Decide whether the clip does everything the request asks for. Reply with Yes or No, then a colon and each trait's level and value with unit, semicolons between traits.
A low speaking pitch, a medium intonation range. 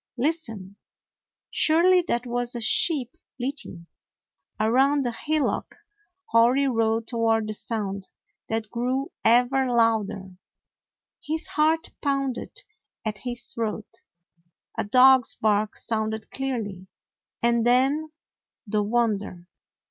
No: high, 235 Hz; average, 3.6 semitones